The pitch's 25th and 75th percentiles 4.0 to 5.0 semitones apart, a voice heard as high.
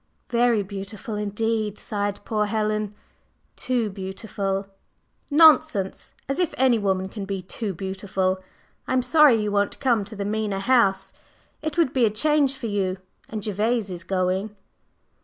No: average, 3.6 semitones; high, 210 Hz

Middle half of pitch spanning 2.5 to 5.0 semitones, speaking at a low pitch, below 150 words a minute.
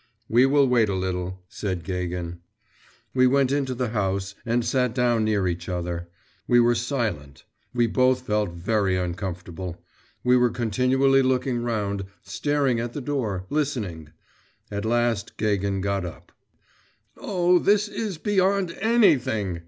No: wide, 5.6 semitones; low, 115 Hz; average, 140 wpm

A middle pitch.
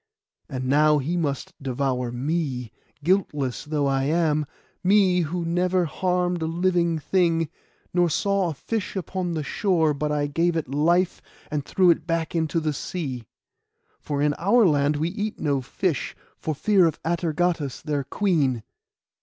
Yes: medium, 160 Hz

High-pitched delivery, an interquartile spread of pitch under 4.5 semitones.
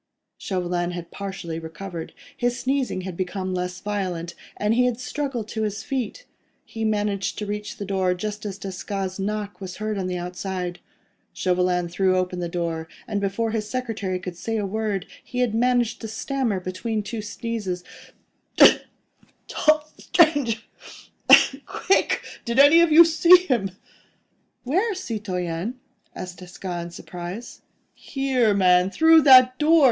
No: high, 205 Hz; average, 5.1 semitones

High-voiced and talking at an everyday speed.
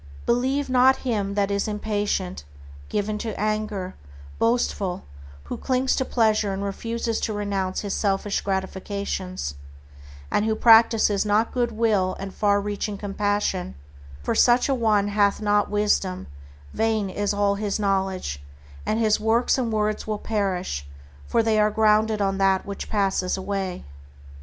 Yes: high, 205 Hz; average, 145 wpm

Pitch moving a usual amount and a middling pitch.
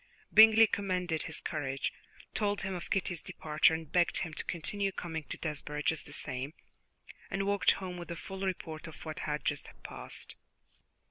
Yes: average, 3.9 semitones; medium, 170 Hz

